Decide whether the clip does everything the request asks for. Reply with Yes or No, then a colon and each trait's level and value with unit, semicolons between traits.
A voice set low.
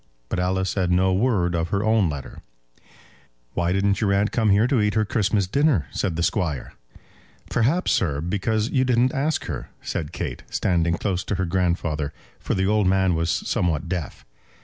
Yes: very low, 95 Hz